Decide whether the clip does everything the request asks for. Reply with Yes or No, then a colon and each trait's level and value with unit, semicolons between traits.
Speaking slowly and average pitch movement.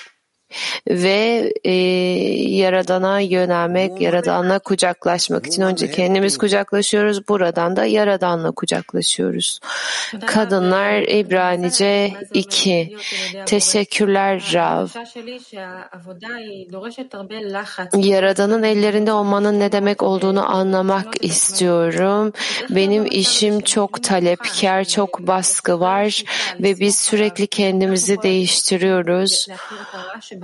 No: slow, 75 wpm; narrow, 2.0 semitones